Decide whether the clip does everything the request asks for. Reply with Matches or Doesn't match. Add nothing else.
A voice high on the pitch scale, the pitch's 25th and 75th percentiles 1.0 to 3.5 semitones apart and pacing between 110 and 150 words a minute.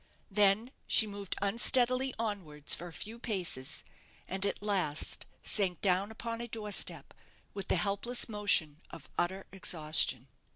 Doesn't match